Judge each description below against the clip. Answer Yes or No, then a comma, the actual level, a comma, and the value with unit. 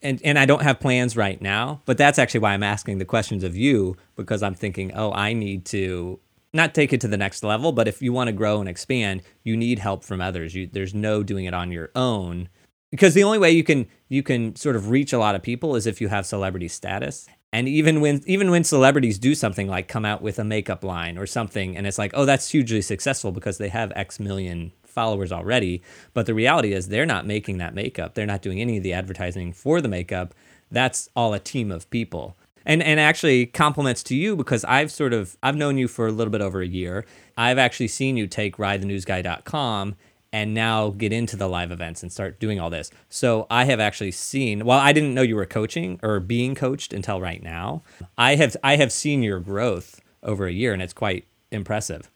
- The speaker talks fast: Yes, fast, 230 wpm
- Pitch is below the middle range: Yes, low, 110 Hz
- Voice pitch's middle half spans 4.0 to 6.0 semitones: Yes, average, 4.8 semitones